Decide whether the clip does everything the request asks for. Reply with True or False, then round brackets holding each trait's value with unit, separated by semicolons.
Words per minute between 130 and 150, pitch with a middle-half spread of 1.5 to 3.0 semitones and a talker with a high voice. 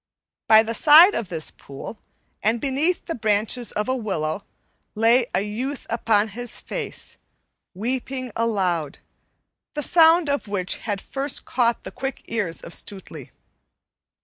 False (140 wpm; 4.6 semitones; 230 Hz)